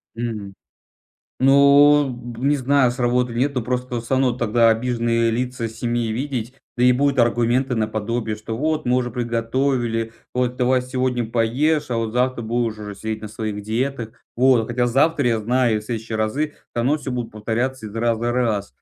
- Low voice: Yes, low, 120 Hz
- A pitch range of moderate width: No, narrow, 2.2 semitones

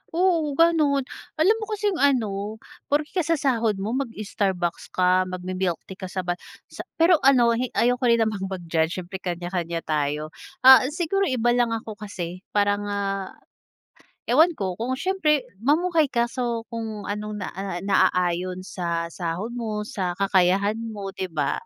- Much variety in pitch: Yes, wide, 5.9 semitones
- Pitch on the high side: Yes, high, 210 Hz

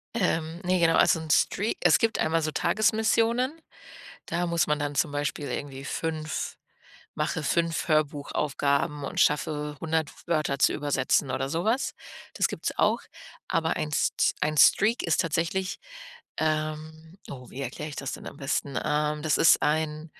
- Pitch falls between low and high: Yes, medium, 155 Hz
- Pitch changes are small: Yes, narrow, 2.3 semitones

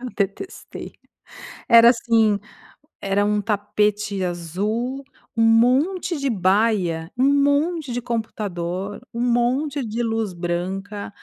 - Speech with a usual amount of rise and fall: Yes, average, 3.8 semitones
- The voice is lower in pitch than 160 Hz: No, high, 220 Hz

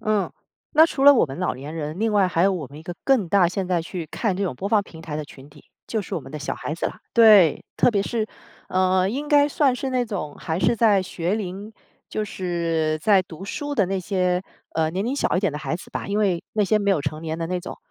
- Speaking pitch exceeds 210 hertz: No, medium, 185 Hz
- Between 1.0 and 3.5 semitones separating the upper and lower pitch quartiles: No, average, 4.6 semitones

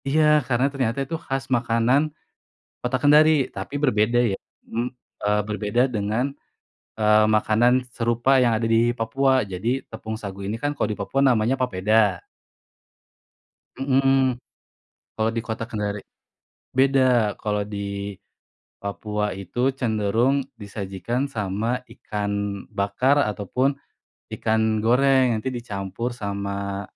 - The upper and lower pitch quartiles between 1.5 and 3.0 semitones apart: No, average, 3.9 semitones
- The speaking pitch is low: Yes, low, 115 Hz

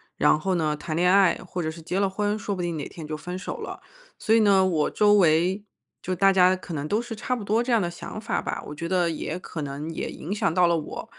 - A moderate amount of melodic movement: Yes, average, 3.8 semitones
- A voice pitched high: No, medium, 180 Hz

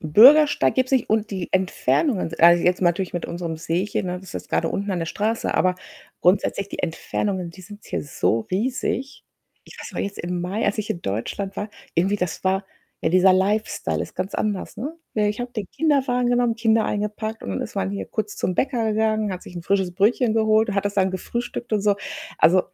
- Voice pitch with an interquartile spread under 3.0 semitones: No, average, 3.4 semitones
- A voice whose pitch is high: Yes, high, 200 Hz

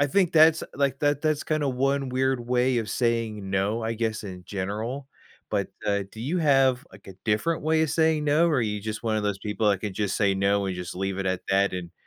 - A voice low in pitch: Yes, low, 115 Hz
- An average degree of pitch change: No, wide, 5.7 semitones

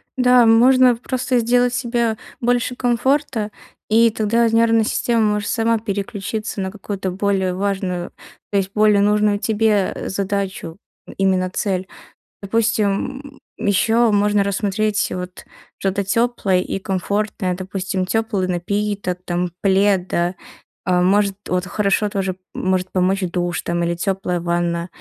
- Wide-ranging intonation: No, average, 3.2 semitones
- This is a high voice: Yes, high, 200 Hz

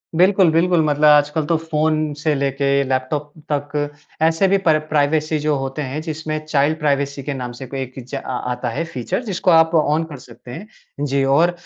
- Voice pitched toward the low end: No, medium, 150 Hz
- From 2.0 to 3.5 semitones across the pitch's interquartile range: Yes, narrow, 2.6 semitones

